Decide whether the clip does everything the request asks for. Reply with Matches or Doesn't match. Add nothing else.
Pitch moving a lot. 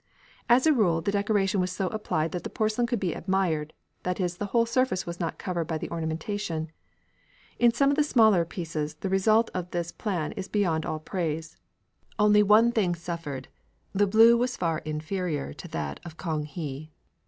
Doesn't match